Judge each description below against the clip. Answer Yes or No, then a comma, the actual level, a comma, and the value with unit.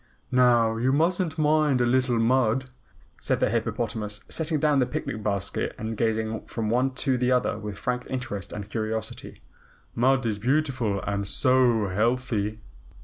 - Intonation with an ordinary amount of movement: Yes, average, 3.2 semitones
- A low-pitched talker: Yes, low, 120 Hz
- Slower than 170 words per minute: Yes, average, 150 wpm